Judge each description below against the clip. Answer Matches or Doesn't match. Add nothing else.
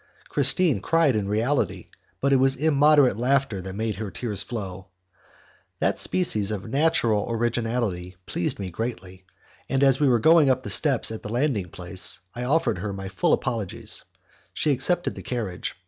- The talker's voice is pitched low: Matches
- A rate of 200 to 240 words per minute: Doesn't match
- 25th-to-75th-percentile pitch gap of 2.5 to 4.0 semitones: Doesn't match